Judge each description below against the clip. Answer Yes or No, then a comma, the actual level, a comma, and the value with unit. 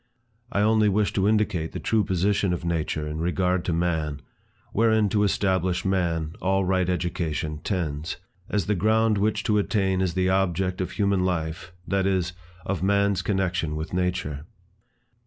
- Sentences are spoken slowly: No, average, 160 wpm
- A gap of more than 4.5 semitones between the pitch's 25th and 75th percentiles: No, average, 2.9 semitones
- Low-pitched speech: Yes, very low, 95 Hz